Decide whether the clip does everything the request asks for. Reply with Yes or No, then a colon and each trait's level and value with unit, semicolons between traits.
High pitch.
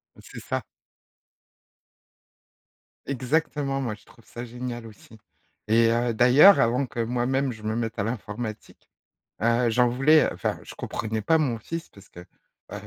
No: low, 120 Hz